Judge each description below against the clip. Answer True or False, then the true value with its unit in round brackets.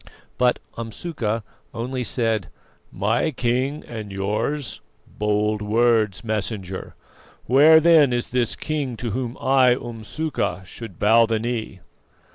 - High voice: False (115 Hz)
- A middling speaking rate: False (115 wpm)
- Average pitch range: True (3.3 semitones)